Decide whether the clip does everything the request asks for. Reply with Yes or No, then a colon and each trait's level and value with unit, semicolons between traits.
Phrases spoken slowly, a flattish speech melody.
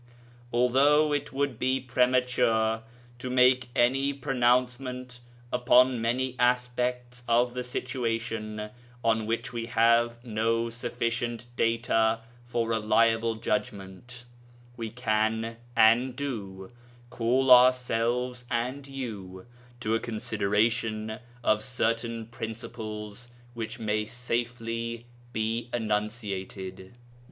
Yes: slow, 100 wpm; narrow, 1.9 semitones